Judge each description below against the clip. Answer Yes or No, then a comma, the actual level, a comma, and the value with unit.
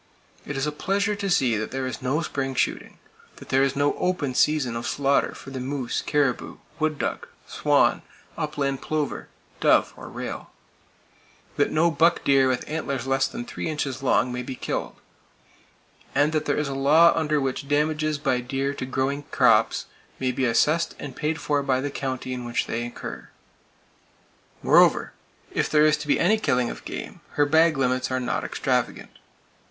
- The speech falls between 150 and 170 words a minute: No, average, 180 wpm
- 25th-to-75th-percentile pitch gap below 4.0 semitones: Yes, average, 2.8 semitones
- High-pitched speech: No, medium, 140 Hz